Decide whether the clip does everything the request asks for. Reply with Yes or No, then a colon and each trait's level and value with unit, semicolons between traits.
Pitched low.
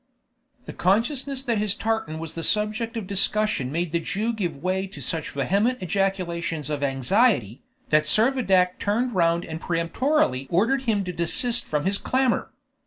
No: high, 190 Hz